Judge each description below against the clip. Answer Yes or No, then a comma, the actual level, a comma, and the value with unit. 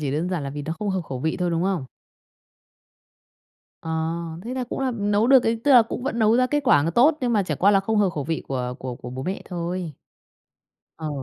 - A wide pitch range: Yes, wide, 6.7 semitones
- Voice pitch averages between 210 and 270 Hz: No, medium, 185 Hz